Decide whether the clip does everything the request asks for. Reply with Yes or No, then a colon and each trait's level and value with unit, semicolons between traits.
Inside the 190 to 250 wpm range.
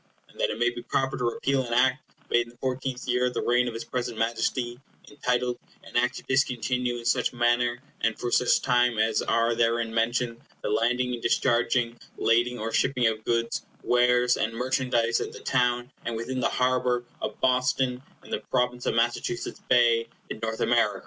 Yes: average, 195 wpm